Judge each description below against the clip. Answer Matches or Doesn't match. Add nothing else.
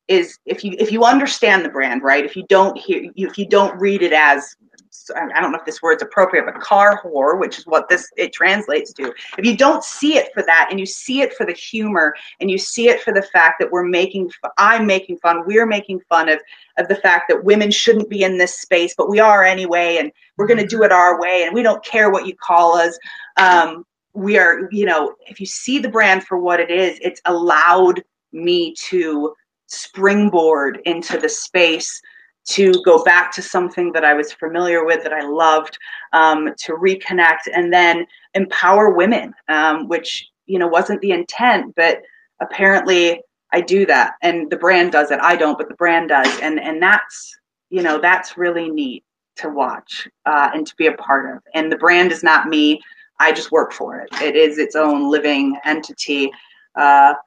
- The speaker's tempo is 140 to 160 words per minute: Doesn't match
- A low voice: Doesn't match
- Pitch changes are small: Doesn't match